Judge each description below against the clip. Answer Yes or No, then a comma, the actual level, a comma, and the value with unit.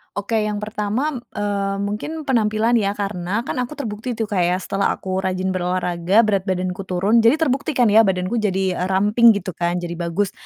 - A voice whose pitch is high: Yes, high, 205 Hz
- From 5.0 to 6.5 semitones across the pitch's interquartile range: No, average, 3.3 semitones